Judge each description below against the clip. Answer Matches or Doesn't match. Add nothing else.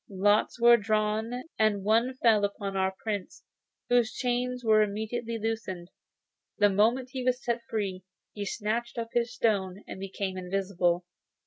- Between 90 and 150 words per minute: Matches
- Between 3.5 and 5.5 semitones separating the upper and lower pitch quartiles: Doesn't match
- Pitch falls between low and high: Doesn't match